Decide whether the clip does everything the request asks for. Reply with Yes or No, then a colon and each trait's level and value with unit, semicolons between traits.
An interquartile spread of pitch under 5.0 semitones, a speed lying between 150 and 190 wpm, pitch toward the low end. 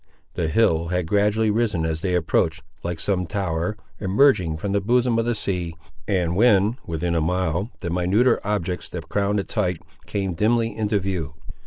Yes: average, 3.8 semitones; average, 175 wpm; very low, 95 Hz